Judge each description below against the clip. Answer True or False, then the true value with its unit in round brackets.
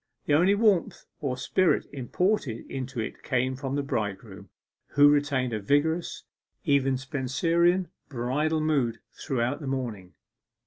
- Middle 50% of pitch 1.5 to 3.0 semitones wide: False (4.1 semitones)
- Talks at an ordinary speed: False (130 wpm)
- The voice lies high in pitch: False (135 Hz)